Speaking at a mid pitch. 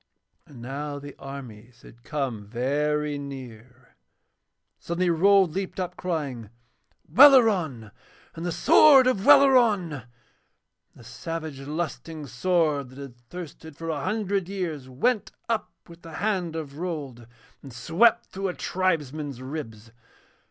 Yes: medium, 155 Hz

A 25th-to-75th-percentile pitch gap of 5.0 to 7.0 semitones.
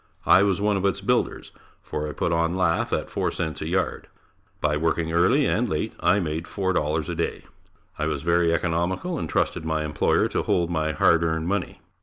No: average, 2.9 semitones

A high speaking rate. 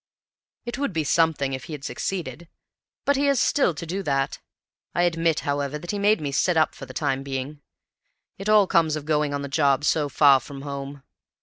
Yes: fast, 210 wpm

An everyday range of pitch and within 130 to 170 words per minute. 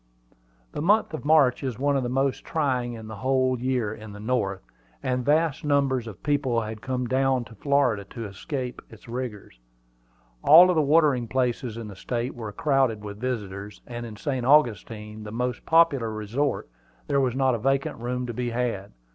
No: average, 3.5 semitones; average, 185 wpm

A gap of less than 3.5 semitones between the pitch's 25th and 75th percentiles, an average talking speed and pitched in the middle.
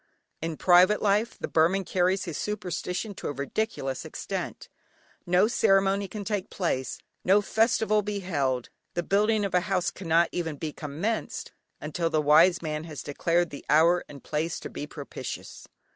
No: average, 4.3 semitones; average, 160 wpm; medium, 180 Hz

